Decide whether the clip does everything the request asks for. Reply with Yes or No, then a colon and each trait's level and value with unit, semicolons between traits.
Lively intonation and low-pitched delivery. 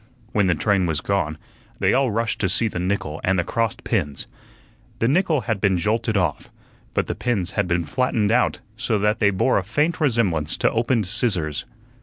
No: average, 4.5 semitones; low, 105 Hz